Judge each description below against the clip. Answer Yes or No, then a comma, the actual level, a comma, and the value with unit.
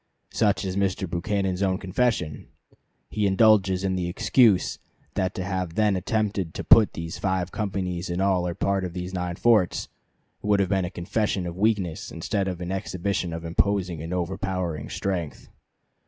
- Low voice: Yes, very low, 95 Hz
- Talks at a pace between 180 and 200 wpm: No, average, 170 wpm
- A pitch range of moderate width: No, narrow, 2.1 semitones